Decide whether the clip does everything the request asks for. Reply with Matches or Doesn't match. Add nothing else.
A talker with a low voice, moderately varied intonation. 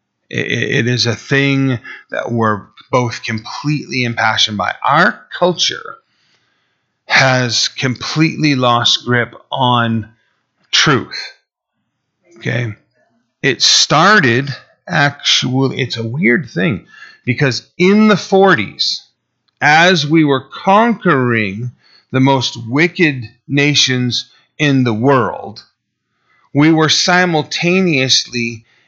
Matches